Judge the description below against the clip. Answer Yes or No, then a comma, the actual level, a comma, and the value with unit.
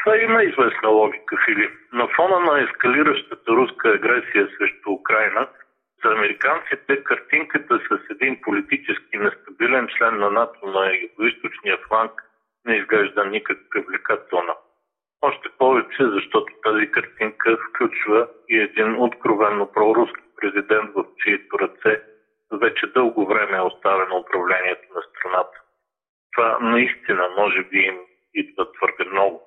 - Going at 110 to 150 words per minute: Yes, average, 120 wpm